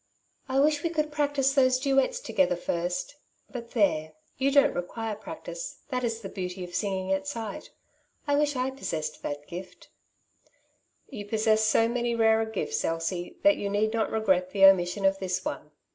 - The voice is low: No, high, 220 Hz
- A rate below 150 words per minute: No, average, 175 wpm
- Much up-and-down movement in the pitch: Yes, wide, 6.2 semitones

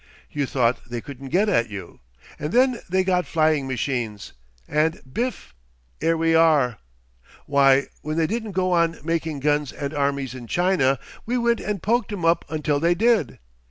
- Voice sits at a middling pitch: Yes, medium, 155 Hz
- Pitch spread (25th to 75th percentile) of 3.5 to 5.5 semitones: Yes, average, 5.0 semitones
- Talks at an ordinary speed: Yes, average, 170 wpm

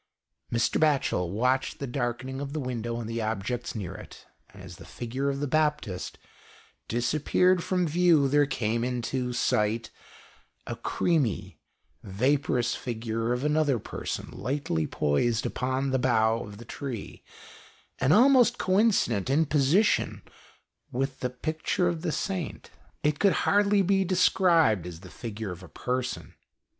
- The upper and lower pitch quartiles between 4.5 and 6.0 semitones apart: Yes, average, 5.2 semitones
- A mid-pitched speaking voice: No, low, 130 Hz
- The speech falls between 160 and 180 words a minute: No, average, 150 wpm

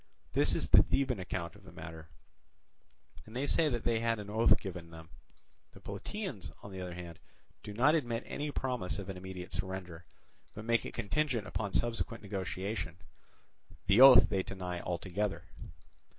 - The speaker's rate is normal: Yes, average, 165 wpm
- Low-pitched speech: Yes, low, 100 Hz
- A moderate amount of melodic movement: Yes, average, 4.5 semitones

